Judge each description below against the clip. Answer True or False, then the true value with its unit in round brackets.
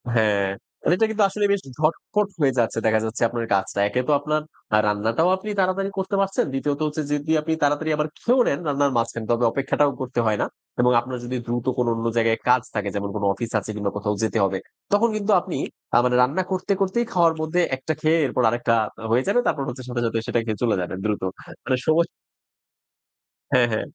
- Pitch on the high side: False (130 Hz)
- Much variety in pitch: True (6.4 semitones)